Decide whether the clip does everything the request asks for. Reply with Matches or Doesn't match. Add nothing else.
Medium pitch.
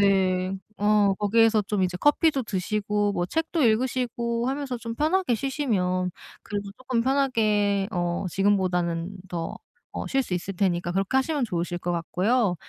Doesn't match